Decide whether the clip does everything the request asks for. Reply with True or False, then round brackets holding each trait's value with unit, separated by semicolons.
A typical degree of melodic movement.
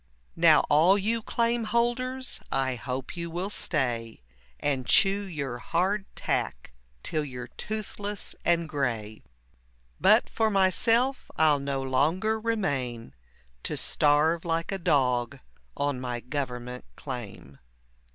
False (8.1 semitones)